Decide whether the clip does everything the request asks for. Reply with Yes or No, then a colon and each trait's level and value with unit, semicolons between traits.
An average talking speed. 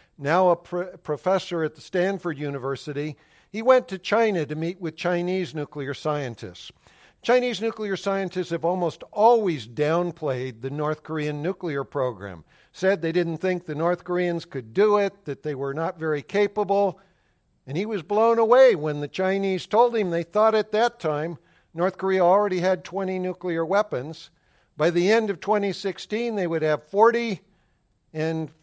Yes: average, 165 wpm